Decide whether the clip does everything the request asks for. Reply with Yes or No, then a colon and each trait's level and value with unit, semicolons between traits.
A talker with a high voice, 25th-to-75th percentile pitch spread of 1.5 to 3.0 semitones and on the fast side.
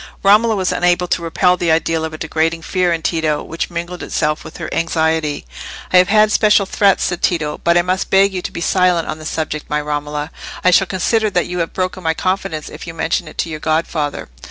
No: medium, 170 Hz; narrow, 2.5 semitones; fast, 230 wpm